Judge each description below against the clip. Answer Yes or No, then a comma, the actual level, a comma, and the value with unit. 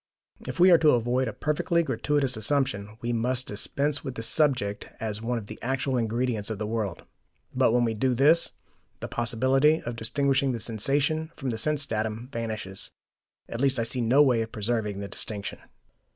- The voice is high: No, low, 120 Hz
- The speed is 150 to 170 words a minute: No, average, 185 wpm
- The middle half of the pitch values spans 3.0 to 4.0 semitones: Yes, average, 3.7 semitones